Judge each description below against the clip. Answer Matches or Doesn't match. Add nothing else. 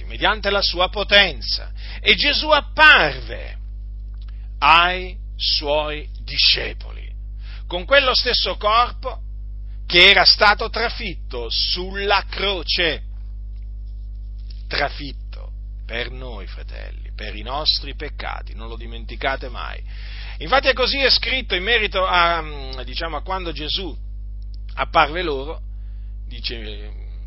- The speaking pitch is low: Matches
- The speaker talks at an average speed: Doesn't match